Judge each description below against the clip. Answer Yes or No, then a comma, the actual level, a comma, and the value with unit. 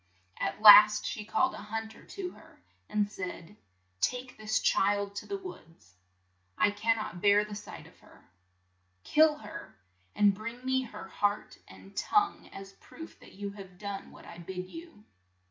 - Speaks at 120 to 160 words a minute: No, average, 180 wpm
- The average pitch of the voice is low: No, high, 205 Hz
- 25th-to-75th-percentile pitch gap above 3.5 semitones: No, average, 3.1 semitones